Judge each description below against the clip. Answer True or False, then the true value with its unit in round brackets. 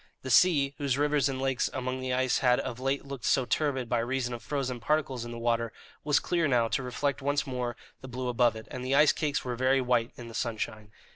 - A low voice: True (130 Hz)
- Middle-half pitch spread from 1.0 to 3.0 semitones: True (2.4 semitones)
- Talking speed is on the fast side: True (235 wpm)